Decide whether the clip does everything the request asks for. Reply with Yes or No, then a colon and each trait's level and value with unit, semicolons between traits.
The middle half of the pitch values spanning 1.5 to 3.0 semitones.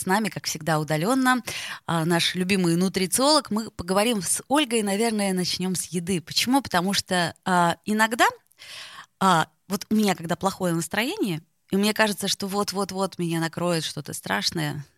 No: average, 3.8 semitones